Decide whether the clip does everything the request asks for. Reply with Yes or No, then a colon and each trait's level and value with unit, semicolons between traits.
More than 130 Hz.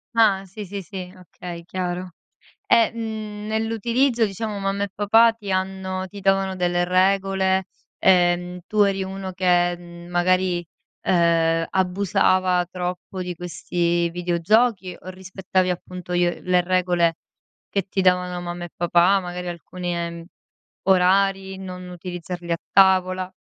Yes: medium, 185 Hz